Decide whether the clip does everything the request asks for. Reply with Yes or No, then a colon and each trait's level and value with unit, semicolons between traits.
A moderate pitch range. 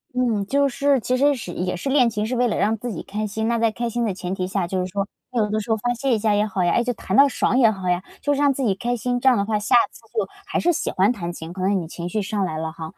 Yes: average, 4.5 semitones